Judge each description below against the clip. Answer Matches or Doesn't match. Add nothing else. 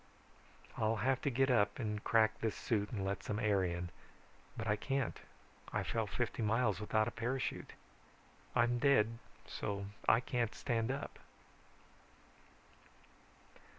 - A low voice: Matches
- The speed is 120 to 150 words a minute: Matches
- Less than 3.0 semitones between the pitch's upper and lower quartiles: Matches